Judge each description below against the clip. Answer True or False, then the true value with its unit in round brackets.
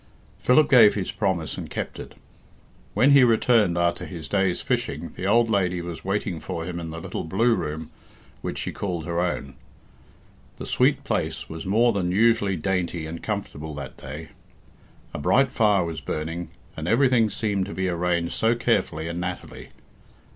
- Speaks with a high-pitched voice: False (90 Hz)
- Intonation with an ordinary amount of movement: True (4.4 semitones)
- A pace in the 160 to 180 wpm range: True (170 wpm)